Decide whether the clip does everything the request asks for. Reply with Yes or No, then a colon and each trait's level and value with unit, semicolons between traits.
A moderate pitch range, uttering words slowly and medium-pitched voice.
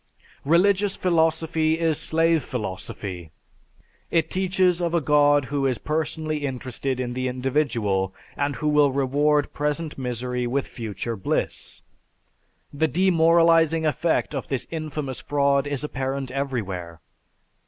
Yes: average, 4.0 semitones; slow, 125 wpm; medium, 145 Hz